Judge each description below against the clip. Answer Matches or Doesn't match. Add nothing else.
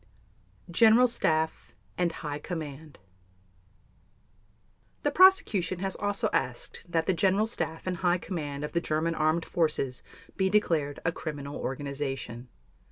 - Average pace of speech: Doesn't match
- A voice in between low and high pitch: Matches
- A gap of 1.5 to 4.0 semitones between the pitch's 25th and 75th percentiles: Doesn't match